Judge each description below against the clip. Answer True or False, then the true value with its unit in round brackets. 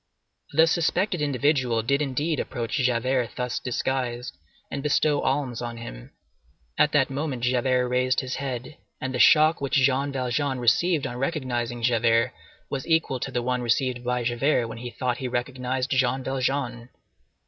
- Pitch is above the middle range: False (130 Hz)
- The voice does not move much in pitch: True (2.3 semitones)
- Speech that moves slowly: False (160 wpm)